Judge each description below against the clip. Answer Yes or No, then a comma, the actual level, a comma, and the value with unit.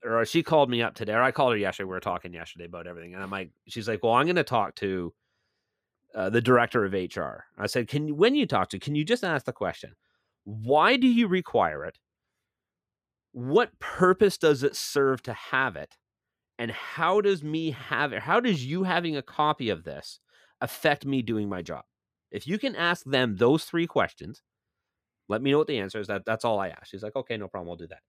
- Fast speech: Yes, fast, 230 wpm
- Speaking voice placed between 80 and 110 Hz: No, low, 120 Hz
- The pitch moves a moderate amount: No, wide, 7.6 semitones